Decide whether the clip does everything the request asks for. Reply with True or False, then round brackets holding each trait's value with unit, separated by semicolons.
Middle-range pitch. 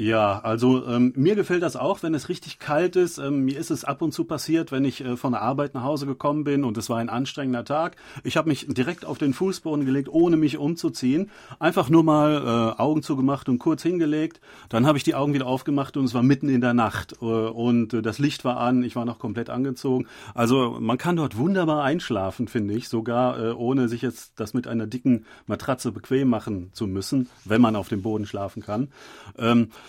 False (130 Hz)